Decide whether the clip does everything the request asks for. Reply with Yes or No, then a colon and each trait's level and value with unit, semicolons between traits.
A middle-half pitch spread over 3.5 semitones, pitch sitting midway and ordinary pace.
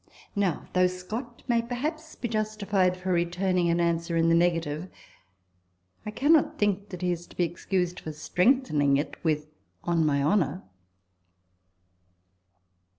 Yes: average, 4.1 semitones; medium, 180 Hz; average, 145 wpm